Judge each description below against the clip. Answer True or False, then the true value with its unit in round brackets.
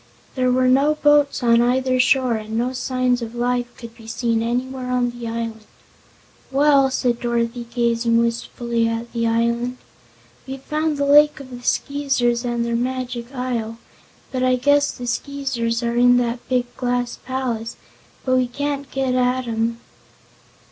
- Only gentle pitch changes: True (1.8 semitones)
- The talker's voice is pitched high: True (245 Hz)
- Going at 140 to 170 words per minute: True (155 wpm)